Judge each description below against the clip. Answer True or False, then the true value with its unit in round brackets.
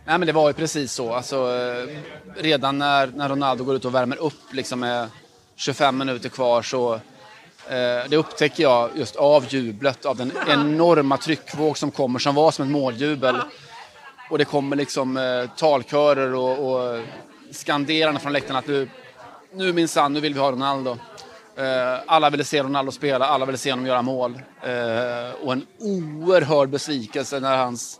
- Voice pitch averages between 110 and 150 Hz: True (140 Hz)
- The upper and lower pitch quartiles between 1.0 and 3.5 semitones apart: True (2.6 semitones)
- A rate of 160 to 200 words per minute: True (170 wpm)